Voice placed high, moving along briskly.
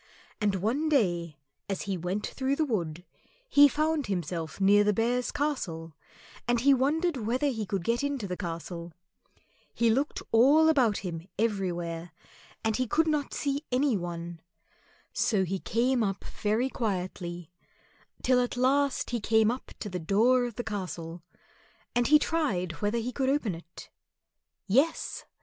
No: high, 220 Hz; average, 155 wpm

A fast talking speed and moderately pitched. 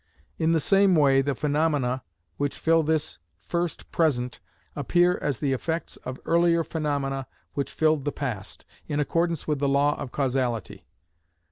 No: average, 150 wpm; medium, 145 Hz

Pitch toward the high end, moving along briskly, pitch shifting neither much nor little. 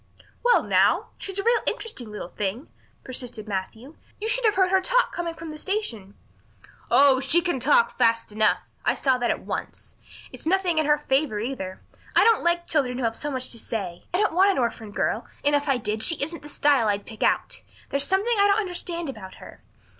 No: very high, 285 Hz; fast, 215 wpm; wide, 7.7 semitones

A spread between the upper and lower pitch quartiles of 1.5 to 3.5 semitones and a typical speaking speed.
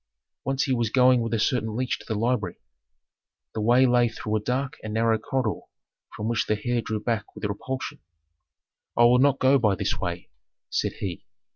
Yes: average, 2.9 semitones; average, 190 wpm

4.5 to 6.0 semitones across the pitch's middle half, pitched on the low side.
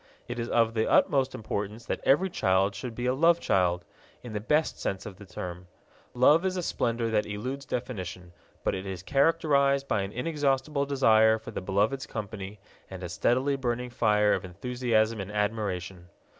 Yes: average, 5.3 semitones; low, 110 Hz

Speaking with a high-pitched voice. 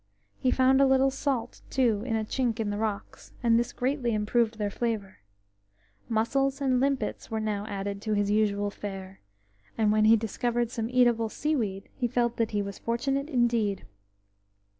Yes: high, 230 Hz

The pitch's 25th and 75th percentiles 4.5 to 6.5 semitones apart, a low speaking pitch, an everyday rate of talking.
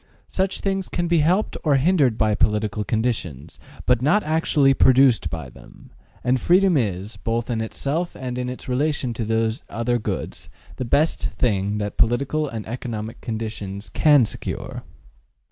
Yes: wide, 5.4 semitones; low, 120 Hz; average, 155 wpm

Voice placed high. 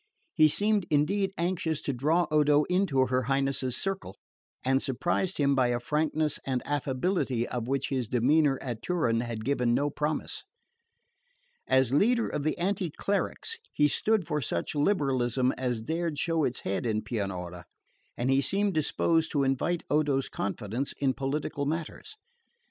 No: medium, 140 Hz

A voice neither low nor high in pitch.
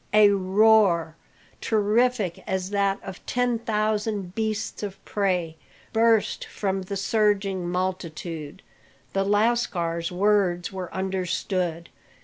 No: high, 195 Hz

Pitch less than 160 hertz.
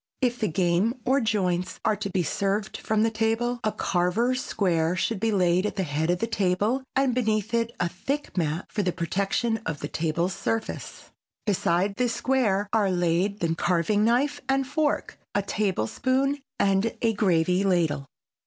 No: high, 200 Hz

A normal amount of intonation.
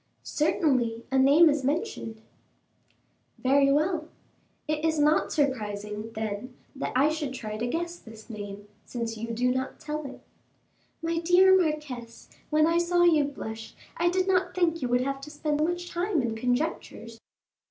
No: wide, 6.0 semitones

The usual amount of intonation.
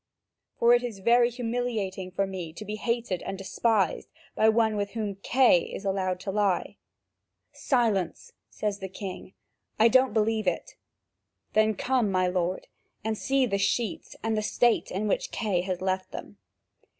Yes: average, 3.5 semitones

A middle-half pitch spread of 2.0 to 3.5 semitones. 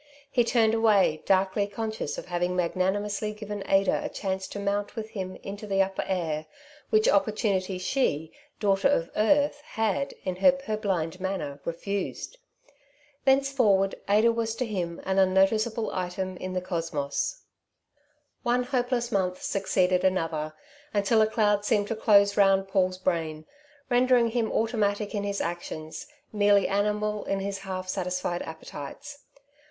Yes: average, 3.1 semitones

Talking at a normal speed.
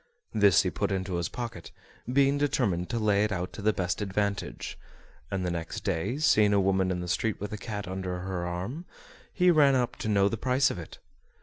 No: fast, 215 wpm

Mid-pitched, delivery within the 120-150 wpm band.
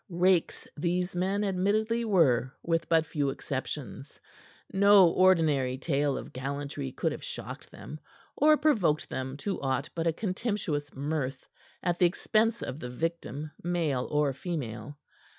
Yes: medium, 165 Hz; average, 140 wpm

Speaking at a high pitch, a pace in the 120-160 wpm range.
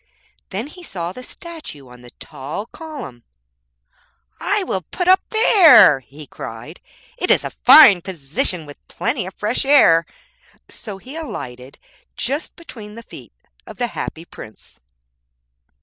Yes: high, 195 Hz; average, 140 wpm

